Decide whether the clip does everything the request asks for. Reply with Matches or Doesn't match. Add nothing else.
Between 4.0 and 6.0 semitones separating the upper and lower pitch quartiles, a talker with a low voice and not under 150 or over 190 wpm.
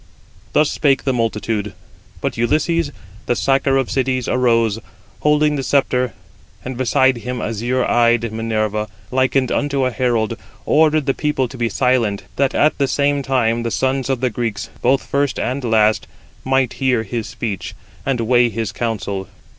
Doesn't match